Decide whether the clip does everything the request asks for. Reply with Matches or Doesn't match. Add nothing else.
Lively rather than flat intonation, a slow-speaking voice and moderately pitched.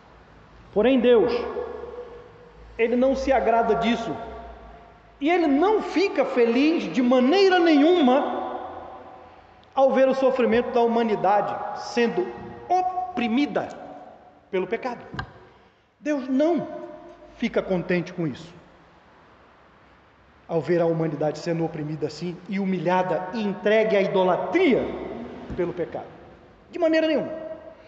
Doesn't match